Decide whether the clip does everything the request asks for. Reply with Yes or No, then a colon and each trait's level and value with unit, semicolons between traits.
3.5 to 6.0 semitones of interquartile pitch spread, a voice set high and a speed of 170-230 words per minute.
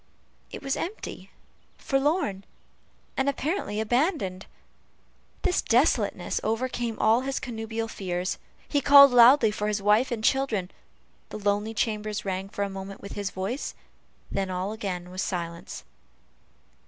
No: average, 4.7 semitones; high, 215 Hz; slow, 135 wpm